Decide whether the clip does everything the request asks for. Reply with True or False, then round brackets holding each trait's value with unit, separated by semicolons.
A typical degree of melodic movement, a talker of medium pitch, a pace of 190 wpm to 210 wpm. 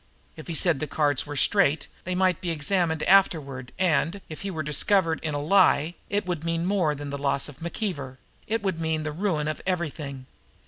True (3.9 semitones; 160 Hz; 200 wpm)